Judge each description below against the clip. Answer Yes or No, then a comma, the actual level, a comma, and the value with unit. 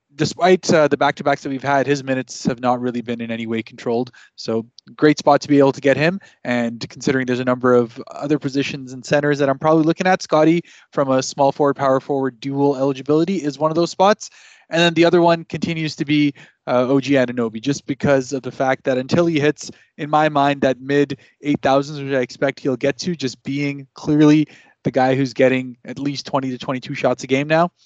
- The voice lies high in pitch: No, medium, 140 Hz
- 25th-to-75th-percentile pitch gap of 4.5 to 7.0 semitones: No, narrow, 2.6 semitones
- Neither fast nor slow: No, fast, 225 wpm